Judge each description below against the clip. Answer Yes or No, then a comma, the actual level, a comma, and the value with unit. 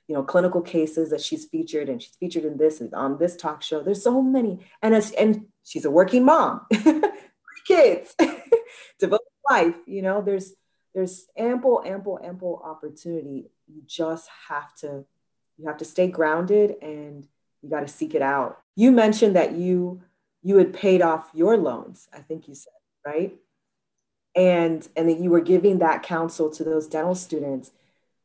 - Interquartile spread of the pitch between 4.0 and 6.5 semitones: Yes, average, 4.8 semitones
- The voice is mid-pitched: Yes, medium, 180 Hz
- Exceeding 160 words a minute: Yes, average, 175 wpm